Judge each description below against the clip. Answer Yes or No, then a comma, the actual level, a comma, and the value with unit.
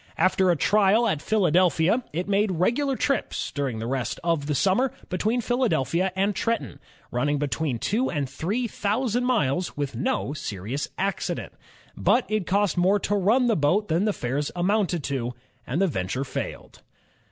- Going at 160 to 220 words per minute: Yes, average, 165 wpm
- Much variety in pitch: Yes, wide, 6.8 semitones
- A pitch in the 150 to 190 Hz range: Yes, medium, 185 Hz